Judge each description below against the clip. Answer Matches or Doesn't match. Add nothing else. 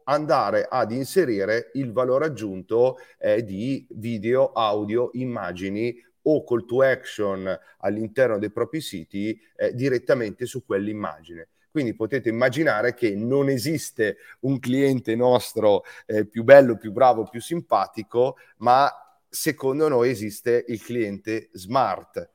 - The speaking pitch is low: Matches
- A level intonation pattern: Doesn't match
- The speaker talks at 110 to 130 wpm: Matches